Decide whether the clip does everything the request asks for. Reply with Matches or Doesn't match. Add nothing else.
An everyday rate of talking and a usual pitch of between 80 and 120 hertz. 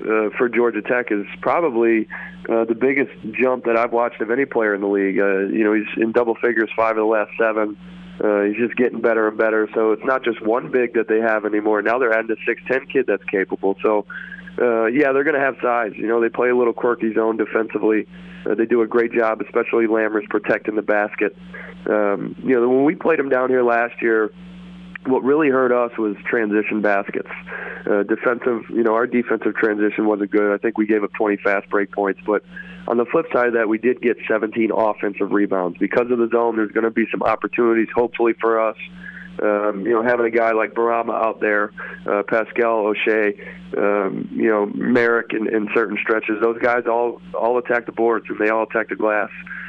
Doesn't match